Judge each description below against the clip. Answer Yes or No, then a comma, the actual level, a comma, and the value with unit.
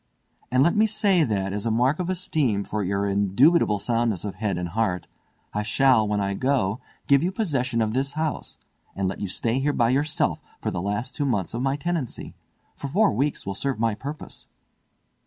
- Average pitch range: No, wide, 5.8 semitones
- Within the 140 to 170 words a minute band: No, average, 200 wpm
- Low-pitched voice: Yes, low, 120 Hz